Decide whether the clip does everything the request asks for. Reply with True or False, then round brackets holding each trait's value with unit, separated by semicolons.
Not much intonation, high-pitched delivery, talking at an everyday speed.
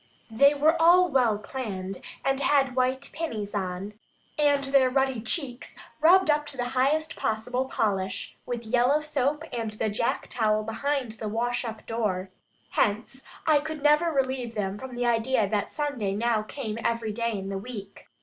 False (4.6 semitones; 245 Hz; 170 wpm)